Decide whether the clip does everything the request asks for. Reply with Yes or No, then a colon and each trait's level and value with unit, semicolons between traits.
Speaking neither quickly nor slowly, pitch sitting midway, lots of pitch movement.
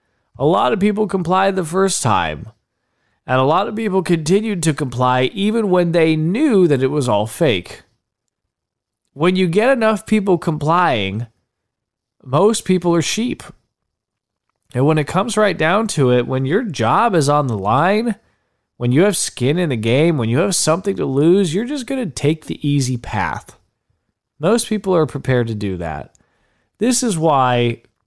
Yes: average, 175 wpm; medium, 160 Hz; wide, 7.6 semitones